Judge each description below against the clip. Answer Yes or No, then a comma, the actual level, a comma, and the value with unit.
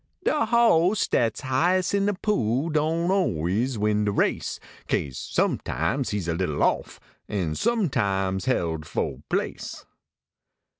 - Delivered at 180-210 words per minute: No, slow, 135 wpm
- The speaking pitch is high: No, low, 120 Hz